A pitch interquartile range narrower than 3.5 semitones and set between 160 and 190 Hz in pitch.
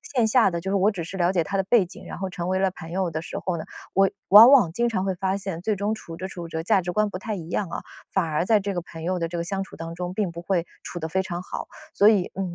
Yes: average, 2.7 semitones; medium, 185 Hz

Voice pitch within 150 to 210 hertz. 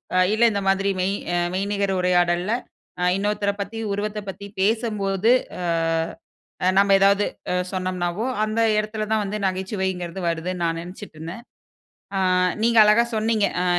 Yes: high, 195 Hz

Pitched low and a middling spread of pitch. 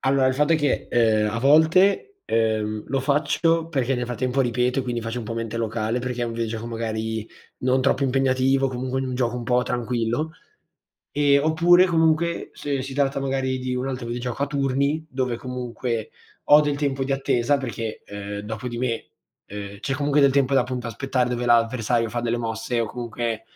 Yes: low, 125 Hz; average, 3.0 semitones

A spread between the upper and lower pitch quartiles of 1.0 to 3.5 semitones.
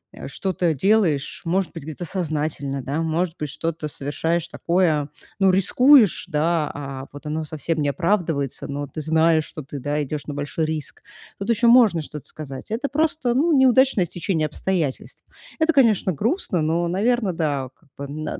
No: average, 4.8 semitones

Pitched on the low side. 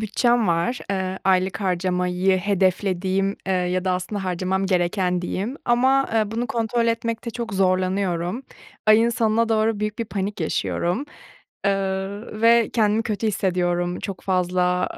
No: high, 195 Hz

